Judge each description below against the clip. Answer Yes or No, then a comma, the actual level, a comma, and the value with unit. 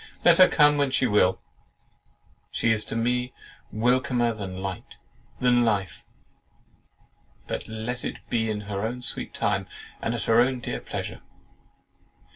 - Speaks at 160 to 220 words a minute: No, average, 145 wpm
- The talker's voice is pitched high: No, low, 115 Hz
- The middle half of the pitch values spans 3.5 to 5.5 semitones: No, average, 2.9 semitones